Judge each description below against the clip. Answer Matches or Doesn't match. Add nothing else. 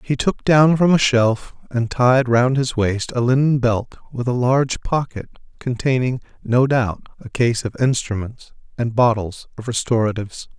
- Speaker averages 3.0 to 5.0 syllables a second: Matches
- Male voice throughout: Matches